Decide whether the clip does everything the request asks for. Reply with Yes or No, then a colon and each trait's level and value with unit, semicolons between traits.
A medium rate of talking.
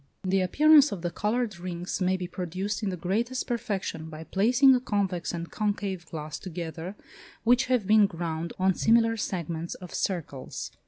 Yes: average, 165 wpm